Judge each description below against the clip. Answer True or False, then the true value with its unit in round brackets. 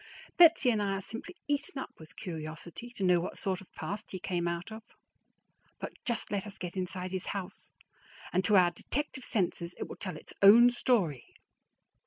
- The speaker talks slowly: False (190 wpm)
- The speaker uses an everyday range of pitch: True (4.3 semitones)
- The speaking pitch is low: False (195 Hz)